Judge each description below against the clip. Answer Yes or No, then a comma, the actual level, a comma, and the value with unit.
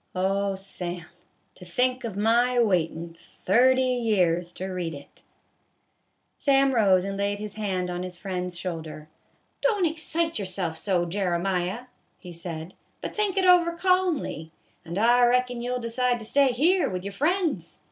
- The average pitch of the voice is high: Yes, high, 200 Hz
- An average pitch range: No, wide, 5.9 semitones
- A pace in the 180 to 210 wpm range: No, average, 165 wpm